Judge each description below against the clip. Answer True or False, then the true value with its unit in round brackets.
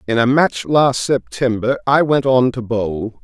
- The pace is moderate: True (185 wpm)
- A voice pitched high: False (125 Hz)